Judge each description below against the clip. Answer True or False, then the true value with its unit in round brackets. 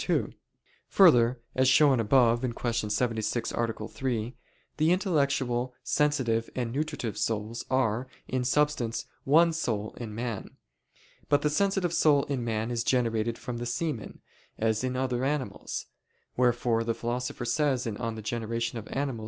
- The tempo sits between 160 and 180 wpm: False (135 wpm)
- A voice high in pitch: False (120 Hz)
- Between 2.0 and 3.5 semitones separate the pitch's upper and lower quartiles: True (3.2 semitones)